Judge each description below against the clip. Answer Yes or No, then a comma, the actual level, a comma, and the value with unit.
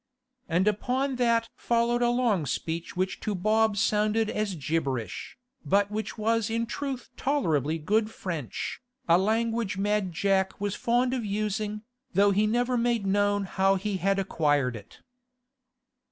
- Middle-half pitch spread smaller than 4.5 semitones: Yes, average, 3.4 semitones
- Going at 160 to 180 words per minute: No, average, 145 wpm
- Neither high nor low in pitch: No, high, 210 Hz